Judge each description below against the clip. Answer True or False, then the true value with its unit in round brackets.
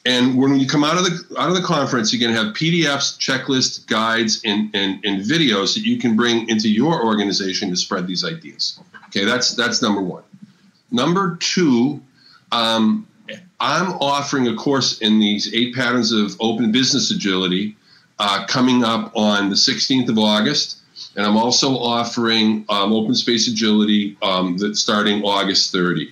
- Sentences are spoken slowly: False (170 wpm)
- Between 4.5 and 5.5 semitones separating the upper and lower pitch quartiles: True (5.1 semitones)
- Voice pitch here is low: True (115 Hz)